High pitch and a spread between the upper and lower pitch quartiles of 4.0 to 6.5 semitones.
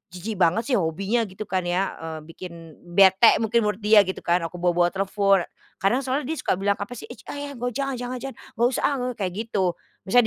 Yes: high, 200 Hz; average, 4.9 semitones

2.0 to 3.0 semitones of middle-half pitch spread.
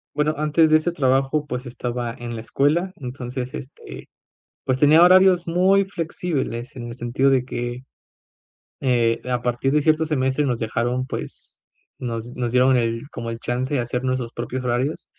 No: average, 3.8 semitones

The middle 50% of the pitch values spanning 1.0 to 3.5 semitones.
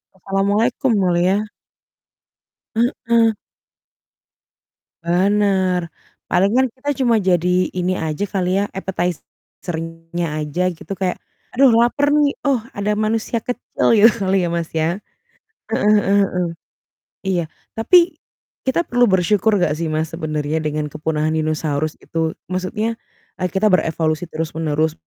No: average, 4.8 semitones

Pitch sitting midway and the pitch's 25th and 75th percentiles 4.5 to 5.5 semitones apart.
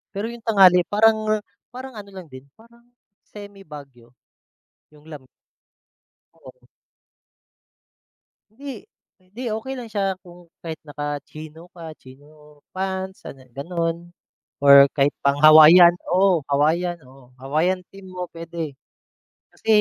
Yes: medium, 170 Hz; average, 5.0 semitones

